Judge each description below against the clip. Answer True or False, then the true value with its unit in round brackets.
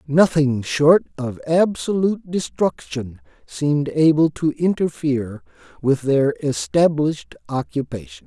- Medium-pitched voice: True (145 Hz)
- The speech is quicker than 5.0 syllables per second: False (4.1 syllables/s)